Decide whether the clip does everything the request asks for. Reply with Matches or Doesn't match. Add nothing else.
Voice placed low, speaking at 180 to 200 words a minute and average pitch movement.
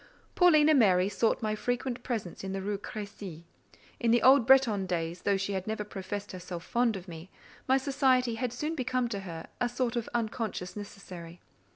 Doesn't match